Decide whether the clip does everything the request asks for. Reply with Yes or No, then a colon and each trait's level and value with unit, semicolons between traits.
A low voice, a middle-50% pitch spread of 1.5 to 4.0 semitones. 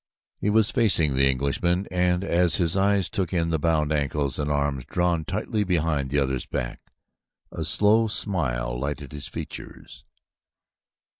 No: very low, 80 Hz; average, 5.0 semitones